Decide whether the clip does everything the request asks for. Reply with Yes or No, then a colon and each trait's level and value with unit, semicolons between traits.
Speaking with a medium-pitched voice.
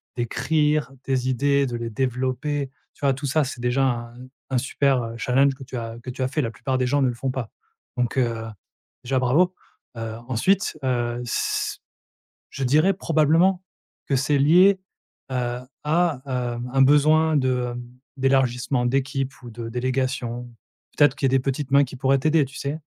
No: low, 130 Hz